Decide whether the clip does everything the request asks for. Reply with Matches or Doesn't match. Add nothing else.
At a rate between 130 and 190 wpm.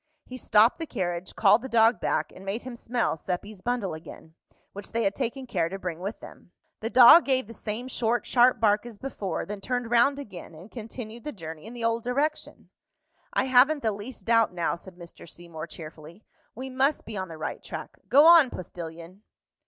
Doesn't match